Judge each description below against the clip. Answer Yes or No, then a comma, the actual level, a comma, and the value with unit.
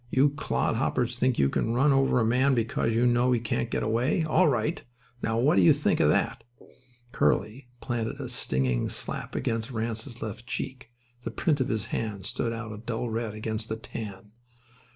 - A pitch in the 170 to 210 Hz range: No, low, 115 Hz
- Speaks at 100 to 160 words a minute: No, average, 190 wpm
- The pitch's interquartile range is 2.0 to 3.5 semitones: Yes, narrow, 2.4 semitones